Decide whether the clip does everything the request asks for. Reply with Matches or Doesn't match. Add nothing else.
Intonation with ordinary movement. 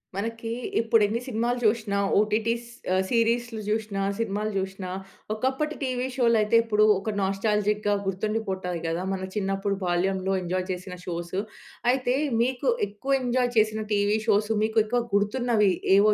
Matches